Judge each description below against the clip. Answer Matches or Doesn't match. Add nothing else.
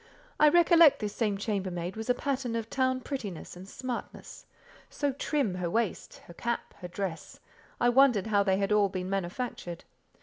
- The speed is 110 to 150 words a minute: Doesn't match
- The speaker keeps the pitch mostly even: Doesn't match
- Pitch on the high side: Matches